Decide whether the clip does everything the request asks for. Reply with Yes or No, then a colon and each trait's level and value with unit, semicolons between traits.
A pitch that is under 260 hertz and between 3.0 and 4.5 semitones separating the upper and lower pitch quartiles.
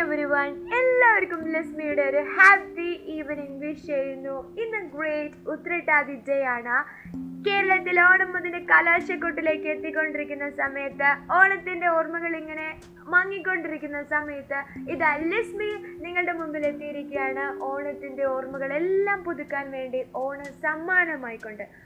No: very high, 310 Hz; average, 4.0 semitones